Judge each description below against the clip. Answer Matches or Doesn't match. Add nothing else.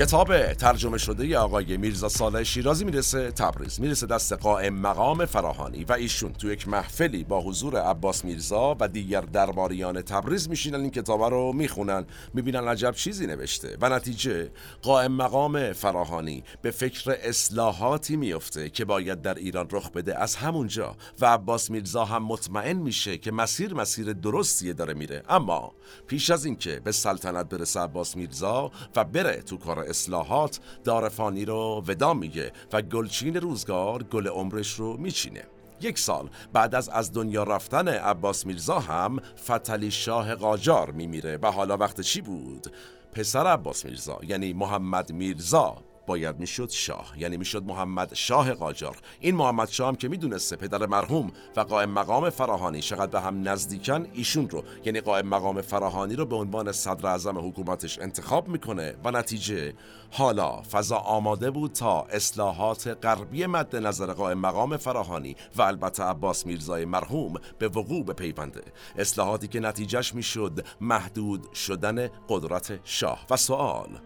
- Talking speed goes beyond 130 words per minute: Matches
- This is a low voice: Matches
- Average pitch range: Matches